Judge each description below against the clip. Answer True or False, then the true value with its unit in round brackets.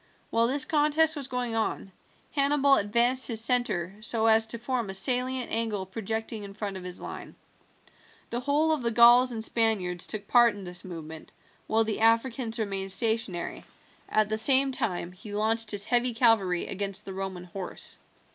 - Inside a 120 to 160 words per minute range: False (175 wpm)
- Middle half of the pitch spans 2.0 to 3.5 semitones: False (3.9 semitones)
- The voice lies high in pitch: True (225 Hz)